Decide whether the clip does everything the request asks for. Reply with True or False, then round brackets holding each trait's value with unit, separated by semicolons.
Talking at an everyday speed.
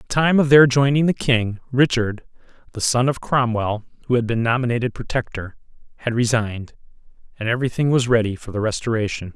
True (180 wpm)